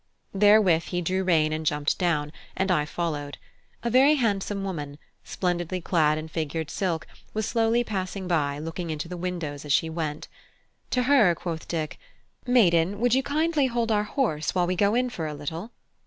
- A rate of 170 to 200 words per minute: Yes, average, 180 wpm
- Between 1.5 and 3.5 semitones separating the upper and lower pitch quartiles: No, average, 5.1 semitones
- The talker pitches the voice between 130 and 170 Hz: No, medium, 180 Hz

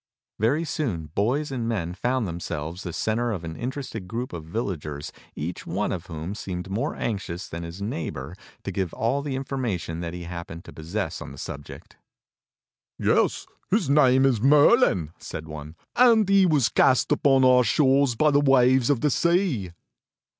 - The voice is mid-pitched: No, low, 110 Hz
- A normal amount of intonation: No, wide, 7.8 semitones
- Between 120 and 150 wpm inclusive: No, average, 170 wpm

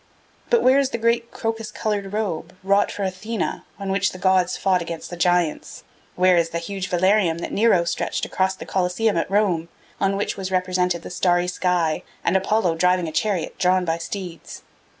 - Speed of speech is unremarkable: Yes, average, 190 wpm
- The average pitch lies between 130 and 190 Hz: Yes, medium, 185 Hz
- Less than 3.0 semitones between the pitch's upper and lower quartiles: Yes, narrow, 2.4 semitones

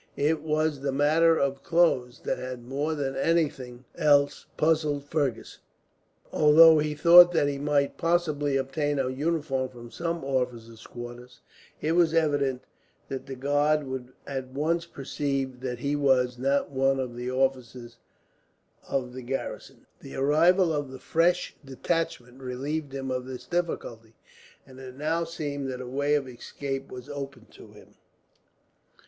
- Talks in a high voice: No, medium, 140 Hz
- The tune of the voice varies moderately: Yes, average, 3.0 semitones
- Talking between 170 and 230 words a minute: No, average, 155 wpm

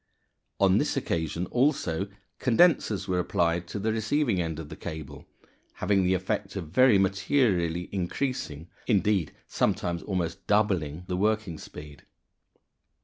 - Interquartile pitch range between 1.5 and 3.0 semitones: No, average, 4.3 semitones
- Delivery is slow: Yes, slow, 130 wpm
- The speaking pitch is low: Yes, very low, 95 Hz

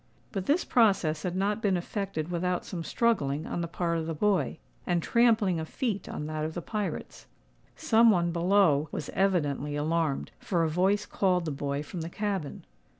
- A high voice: No, medium, 175 Hz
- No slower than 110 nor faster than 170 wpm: No, average, 185 wpm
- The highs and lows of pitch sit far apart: No, average, 4.1 semitones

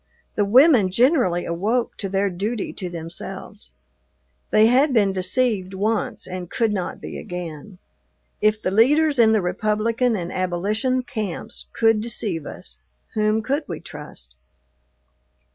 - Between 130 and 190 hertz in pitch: No, high, 210 Hz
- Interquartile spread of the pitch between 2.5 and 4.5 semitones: Yes, average, 4.2 semitones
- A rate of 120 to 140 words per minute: Yes, slow, 135 wpm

